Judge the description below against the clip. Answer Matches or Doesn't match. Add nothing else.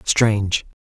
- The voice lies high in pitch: Doesn't match